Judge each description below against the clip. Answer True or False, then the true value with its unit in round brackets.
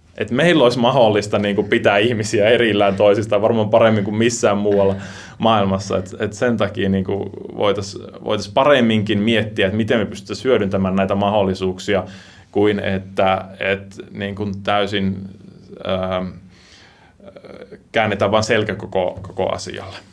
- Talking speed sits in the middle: True (125 wpm)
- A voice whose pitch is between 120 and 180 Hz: False (100 Hz)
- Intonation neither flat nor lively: False (1.9 semitones)